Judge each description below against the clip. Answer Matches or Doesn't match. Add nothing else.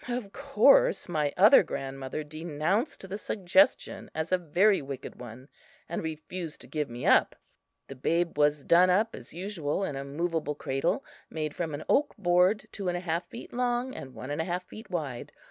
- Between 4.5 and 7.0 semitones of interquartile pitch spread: Matches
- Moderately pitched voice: Matches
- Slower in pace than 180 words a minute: Doesn't match